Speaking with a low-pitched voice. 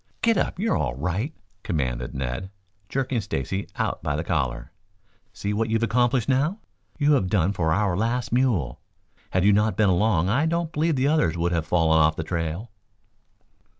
Yes: low, 100 Hz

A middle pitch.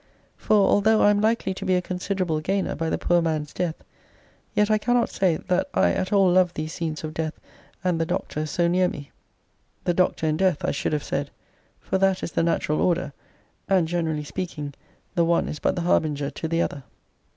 Yes: medium, 175 Hz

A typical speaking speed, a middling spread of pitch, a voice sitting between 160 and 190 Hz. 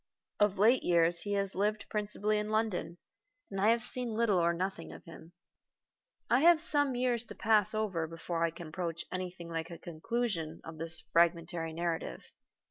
Yes: average, 180 wpm; average, 4.5 semitones; medium, 185 Hz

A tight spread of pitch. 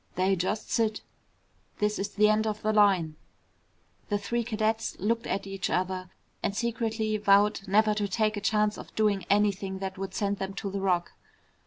Yes: narrow, 1.8 semitones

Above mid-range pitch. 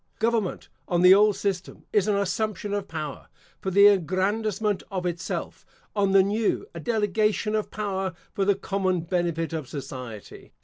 Yes: high, 195 Hz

